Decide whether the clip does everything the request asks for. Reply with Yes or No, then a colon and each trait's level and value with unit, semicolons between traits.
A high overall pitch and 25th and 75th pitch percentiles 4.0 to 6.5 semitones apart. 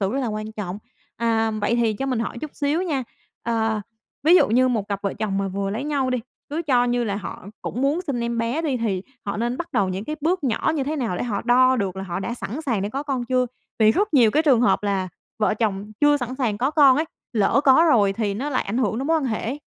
Yes: high, 240 Hz; average, 4.7 semitones